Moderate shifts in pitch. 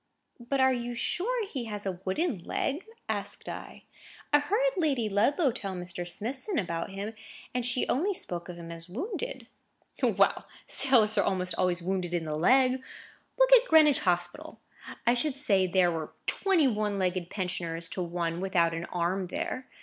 No: wide, 7.7 semitones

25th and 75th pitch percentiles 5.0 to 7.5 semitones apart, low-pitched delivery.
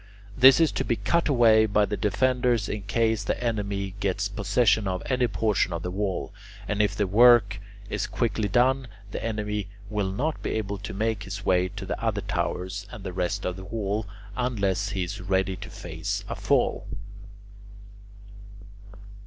No: average, 2.8 semitones; low, 105 Hz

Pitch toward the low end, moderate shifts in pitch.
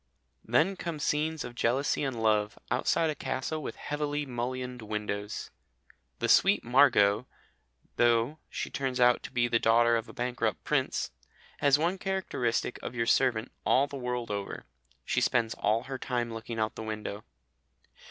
Yes: low, 125 Hz; average, 3.7 semitones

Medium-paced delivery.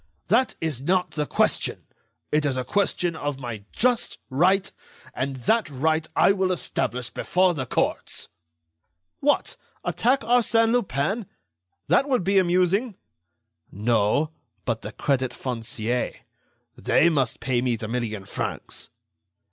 No: slow, 130 wpm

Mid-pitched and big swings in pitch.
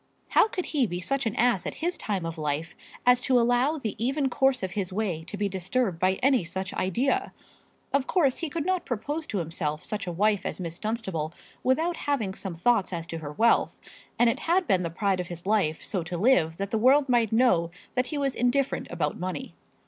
No: high, 215 Hz; wide, 6.7 semitones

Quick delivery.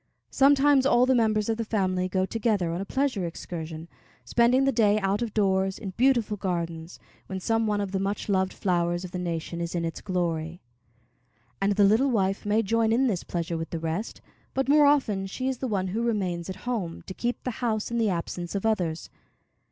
Yes: fast, 210 wpm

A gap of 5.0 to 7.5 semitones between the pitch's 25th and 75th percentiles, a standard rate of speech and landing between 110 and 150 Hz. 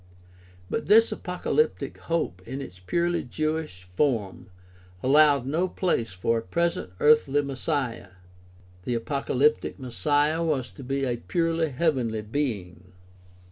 No: wide, 5.5 semitones; slow, 120 wpm; medium, 140 Hz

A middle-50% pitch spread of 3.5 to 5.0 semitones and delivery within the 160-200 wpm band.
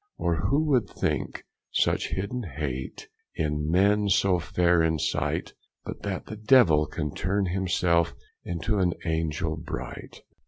No: average, 3.8 semitones; average, 145 wpm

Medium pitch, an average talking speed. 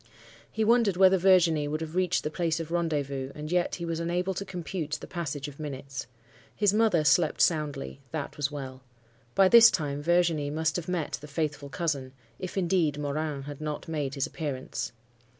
Yes: medium, 155 Hz; average, 185 wpm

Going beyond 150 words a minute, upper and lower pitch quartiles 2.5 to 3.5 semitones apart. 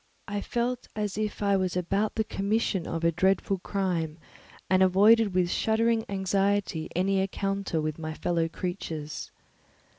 No: average, 145 wpm; average, 2.9 semitones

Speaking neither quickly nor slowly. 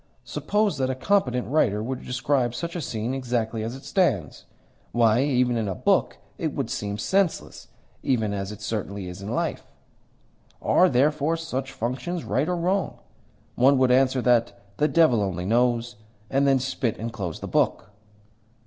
Yes: average, 170 wpm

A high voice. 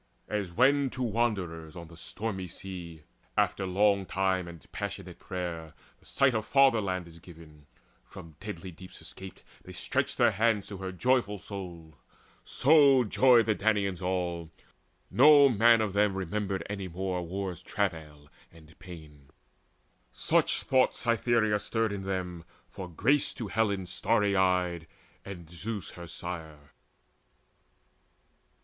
No: very low, 95 Hz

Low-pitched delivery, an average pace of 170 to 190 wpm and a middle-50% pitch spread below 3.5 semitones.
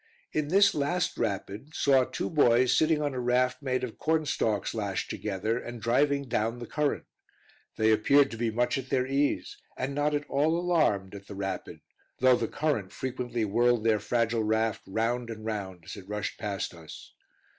No: low, 120 Hz; average, 180 wpm; average, 4.6 semitones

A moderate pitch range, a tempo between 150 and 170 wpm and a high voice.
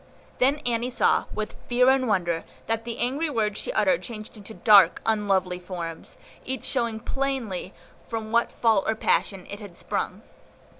Yes: average, 3.8 semitones; average, 160 wpm; high, 220 Hz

